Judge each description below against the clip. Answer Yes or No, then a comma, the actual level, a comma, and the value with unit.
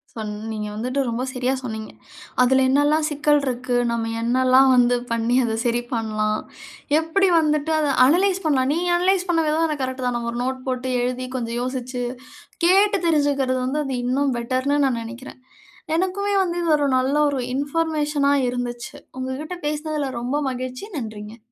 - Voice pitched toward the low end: No, very high, 260 Hz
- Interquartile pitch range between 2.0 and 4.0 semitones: Yes, average, 3.6 semitones